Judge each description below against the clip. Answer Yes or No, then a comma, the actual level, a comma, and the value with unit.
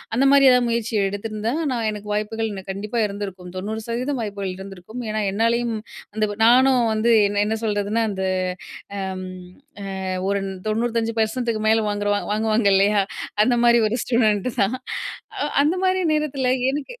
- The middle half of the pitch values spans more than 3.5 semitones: No, average, 2.7 semitones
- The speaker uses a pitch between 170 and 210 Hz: No, high, 220 Hz